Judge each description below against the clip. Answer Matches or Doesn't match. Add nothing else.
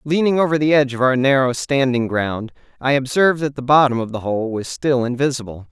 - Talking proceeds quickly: Matches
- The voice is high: Doesn't match